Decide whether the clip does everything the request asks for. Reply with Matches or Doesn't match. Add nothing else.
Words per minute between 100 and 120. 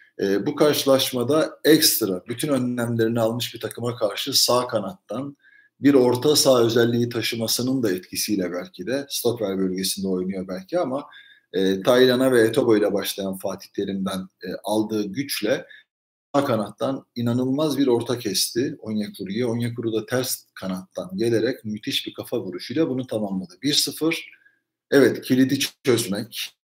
Doesn't match